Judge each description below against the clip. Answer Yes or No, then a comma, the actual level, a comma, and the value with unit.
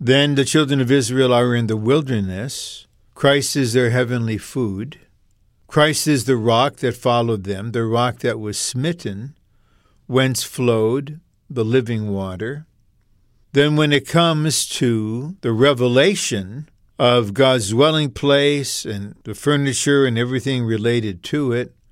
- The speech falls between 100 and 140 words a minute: Yes, slow, 135 wpm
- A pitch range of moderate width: Yes, average, 3.8 semitones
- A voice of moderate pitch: No, low, 125 Hz